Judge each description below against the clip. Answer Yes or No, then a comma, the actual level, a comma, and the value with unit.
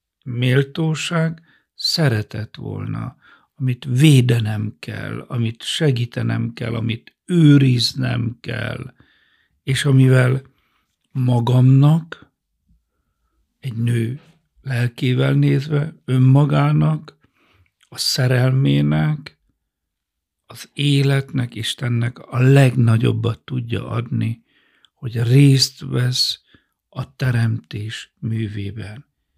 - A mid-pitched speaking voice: No, low, 125 Hz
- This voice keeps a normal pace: No, slow, 70 wpm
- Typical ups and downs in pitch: Yes, average, 3.1 semitones